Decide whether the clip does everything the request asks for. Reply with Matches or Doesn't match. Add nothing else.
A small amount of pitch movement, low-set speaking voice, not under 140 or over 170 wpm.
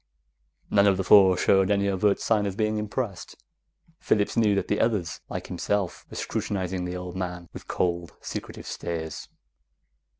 Matches